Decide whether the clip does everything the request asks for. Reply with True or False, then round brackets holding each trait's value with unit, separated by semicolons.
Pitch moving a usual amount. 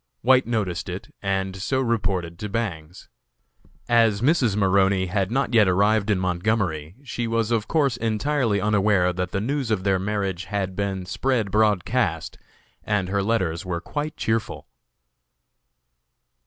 True (3.5 semitones)